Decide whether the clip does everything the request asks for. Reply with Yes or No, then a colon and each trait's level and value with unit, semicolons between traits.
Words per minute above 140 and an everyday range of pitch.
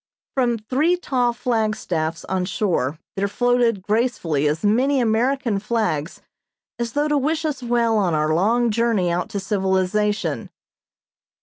No: slow, 135 wpm; average, 4.5 semitones